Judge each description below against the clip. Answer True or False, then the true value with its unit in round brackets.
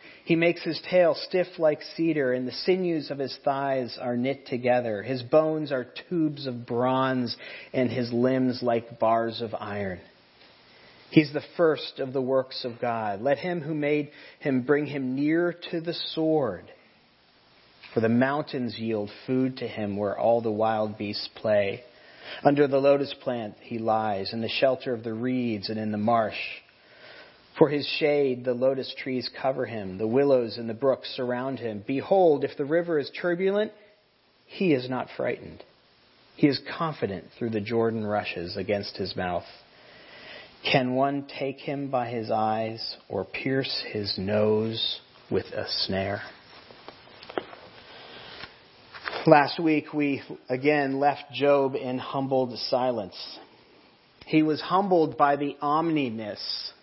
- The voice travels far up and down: False (4.2 semitones)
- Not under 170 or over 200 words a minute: False (150 wpm)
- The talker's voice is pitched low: True (130 Hz)